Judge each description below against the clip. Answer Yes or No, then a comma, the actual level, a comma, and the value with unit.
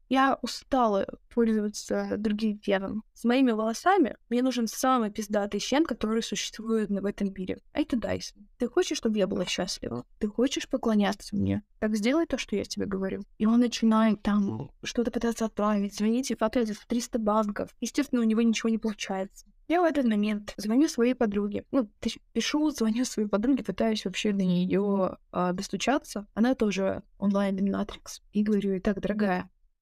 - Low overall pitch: No, high, 220 Hz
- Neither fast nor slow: No, fast, 165 wpm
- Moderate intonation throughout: Yes, average, 3.3 semitones